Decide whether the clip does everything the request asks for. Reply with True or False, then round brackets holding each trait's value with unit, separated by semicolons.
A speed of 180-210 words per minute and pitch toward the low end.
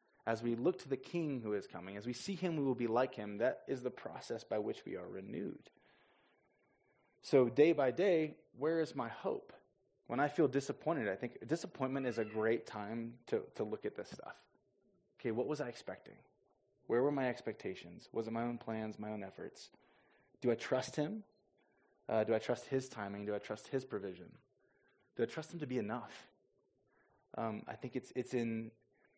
True (200 wpm; 125 Hz)